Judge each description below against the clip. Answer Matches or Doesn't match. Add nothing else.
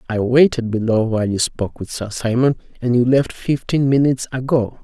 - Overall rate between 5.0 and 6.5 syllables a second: Matches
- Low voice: Matches